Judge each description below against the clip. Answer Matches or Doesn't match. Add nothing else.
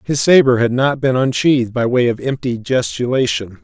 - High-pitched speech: Doesn't match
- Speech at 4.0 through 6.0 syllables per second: Matches